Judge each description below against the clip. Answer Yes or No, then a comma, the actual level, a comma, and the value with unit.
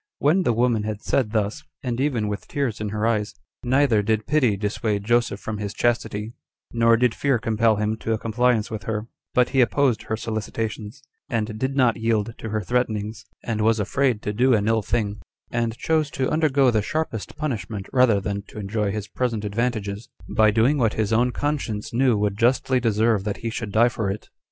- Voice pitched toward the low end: Yes, low, 115 Hz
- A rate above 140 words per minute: Yes, average, 200 wpm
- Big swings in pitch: No, average, 2.7 semitones